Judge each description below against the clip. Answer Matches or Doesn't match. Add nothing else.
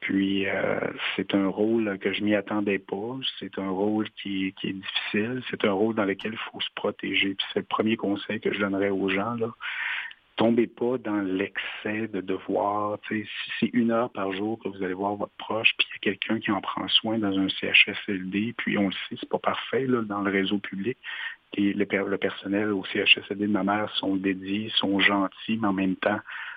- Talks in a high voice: Doesn't match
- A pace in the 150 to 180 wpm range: Doesn't match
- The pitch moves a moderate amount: Doesn't match